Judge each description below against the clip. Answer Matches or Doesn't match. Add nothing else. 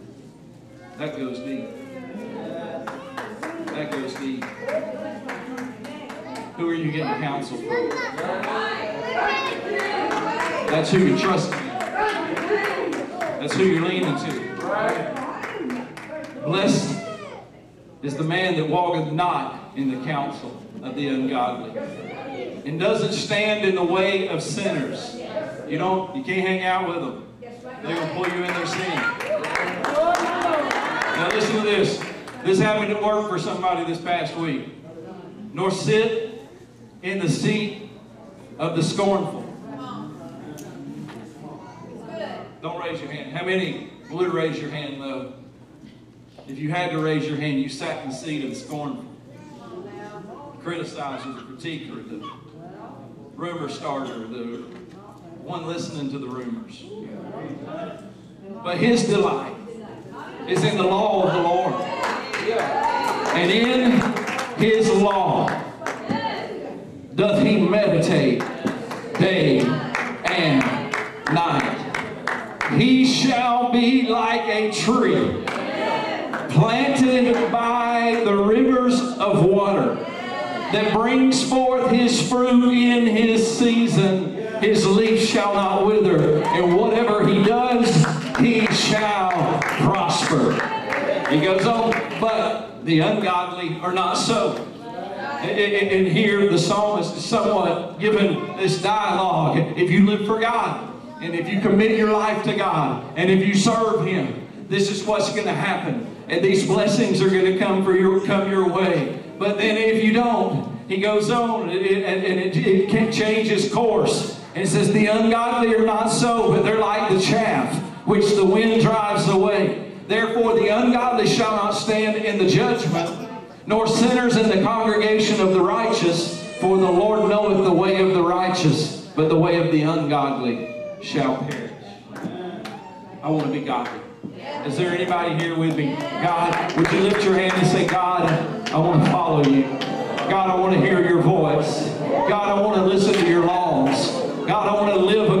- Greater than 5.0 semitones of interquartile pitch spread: Doesn't match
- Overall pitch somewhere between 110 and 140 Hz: Doesn't match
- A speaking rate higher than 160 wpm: Doesn't match